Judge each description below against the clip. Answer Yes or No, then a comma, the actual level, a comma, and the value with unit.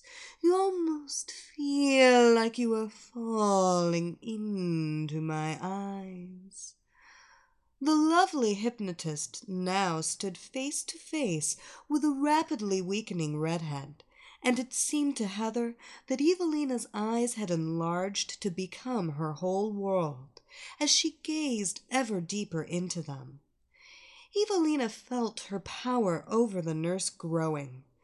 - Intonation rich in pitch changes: Yes, wide, 8.5 semitones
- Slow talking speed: Yes, slow, 115 wpm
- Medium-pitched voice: No, high, 215 Hz